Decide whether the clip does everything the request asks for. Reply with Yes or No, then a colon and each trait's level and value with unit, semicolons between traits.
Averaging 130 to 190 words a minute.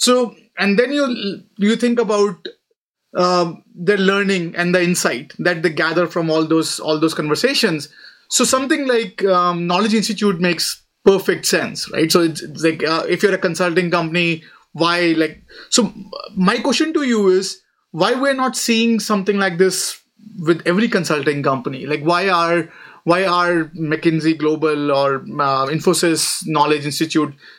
Yes: average, 160 wpm